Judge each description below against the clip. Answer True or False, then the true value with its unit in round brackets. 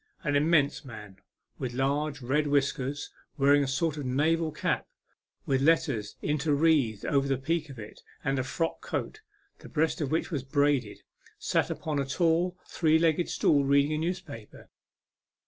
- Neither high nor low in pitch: True (145 Hz)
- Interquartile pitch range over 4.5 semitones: False (2.9 semitones)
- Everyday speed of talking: True (165 wpm)